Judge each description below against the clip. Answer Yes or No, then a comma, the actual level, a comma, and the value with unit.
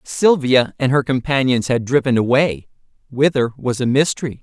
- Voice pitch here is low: Yes, low, 130 Hz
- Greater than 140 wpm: No, slow, 135 wpm